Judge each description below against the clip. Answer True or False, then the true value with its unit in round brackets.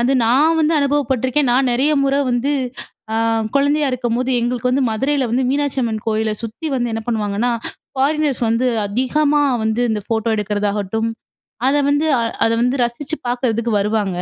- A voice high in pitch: True (245 Hz)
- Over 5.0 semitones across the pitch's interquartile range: False (3.9 semitones)